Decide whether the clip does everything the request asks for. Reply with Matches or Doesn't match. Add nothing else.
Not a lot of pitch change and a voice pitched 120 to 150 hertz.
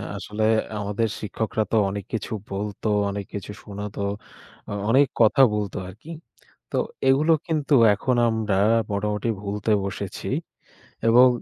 Doesn't match